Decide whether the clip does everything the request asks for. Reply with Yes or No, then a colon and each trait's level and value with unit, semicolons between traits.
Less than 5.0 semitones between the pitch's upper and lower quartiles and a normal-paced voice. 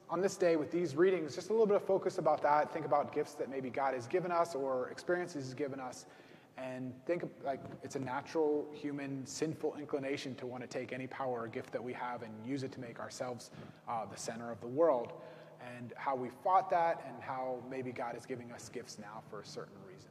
No: average, 4.2 semitones; fast, 235 wpm